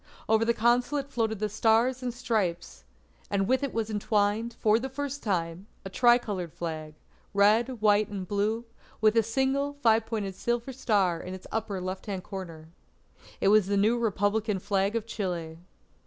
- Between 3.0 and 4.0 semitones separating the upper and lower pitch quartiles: Yes, average, 3.5 semitones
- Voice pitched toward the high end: Yes, high, 215 Hz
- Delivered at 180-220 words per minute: No, average, 170 wpm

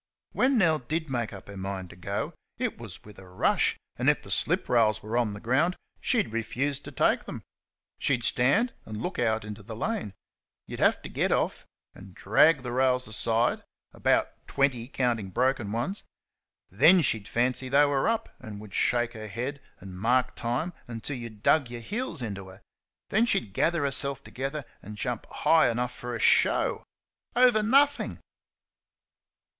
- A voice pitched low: Yes, low, 120 Hz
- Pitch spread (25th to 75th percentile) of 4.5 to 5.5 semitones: Yes, average, 5.2 semitones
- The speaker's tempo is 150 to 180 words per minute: Yes, average, 175 wpm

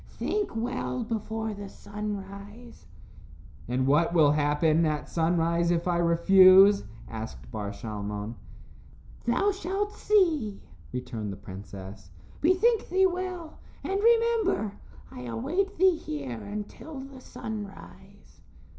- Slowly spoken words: Yes, slow, 110 wpm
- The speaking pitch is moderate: No, high, 200 Hz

